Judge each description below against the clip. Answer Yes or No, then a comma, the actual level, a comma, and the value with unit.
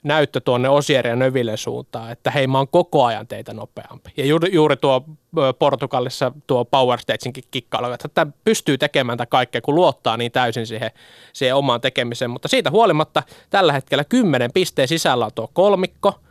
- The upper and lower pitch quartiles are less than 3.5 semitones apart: No, average, 3.8 semitones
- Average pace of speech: No, fast, 170 wpm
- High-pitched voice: No, medium, 140 Hz